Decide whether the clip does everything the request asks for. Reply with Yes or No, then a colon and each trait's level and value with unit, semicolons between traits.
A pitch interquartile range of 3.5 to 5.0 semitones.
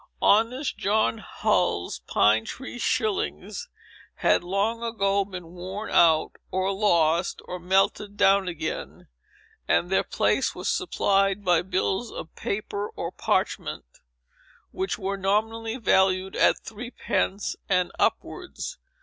No: average, 3.0 semitones